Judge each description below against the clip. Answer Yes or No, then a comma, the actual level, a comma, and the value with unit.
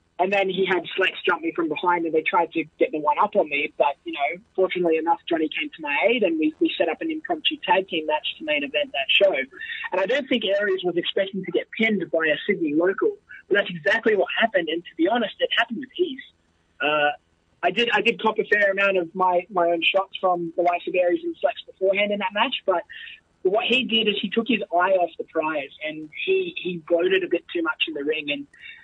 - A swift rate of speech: Yes, fast, 250 wpm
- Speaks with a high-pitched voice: Yes, high, 200 Hz